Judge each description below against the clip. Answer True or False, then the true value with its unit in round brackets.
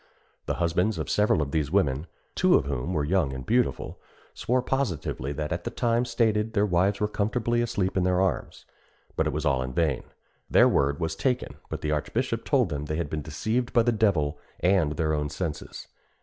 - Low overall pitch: True (85 Hz)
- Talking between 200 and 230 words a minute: True (205 wpm)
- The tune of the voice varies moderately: False (6.7 semitones)